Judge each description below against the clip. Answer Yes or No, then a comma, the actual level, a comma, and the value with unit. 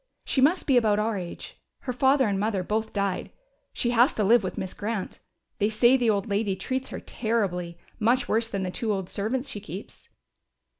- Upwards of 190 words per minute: Yes, fast, 205 wpm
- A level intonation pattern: No, average, 3.5 semitones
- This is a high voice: Yes, high, 215 Hz